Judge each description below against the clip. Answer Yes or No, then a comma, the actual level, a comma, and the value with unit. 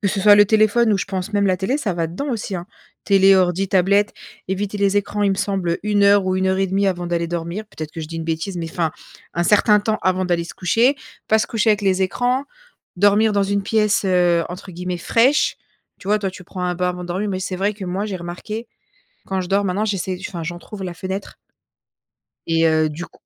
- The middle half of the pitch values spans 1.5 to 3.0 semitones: Yes, narrow, 2.5 semitones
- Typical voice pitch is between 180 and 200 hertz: Yes, high, 190 Hz